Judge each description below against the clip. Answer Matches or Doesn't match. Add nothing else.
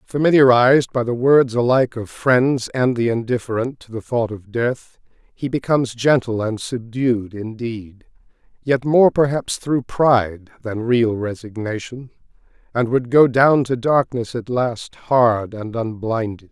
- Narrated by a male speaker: Matches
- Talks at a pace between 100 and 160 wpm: Matches